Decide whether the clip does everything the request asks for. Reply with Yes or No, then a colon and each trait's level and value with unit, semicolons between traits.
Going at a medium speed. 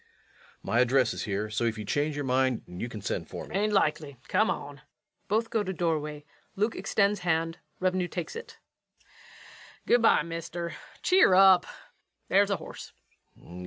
Yes: average, 170 wpm